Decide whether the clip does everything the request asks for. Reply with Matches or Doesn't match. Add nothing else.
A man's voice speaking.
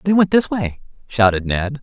Matches